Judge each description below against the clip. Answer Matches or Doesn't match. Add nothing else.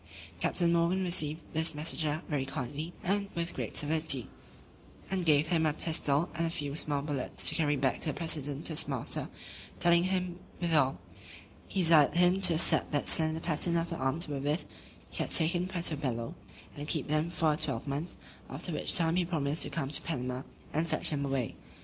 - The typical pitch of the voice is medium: Matches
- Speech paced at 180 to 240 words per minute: Matches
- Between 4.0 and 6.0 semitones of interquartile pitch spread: Doesn't match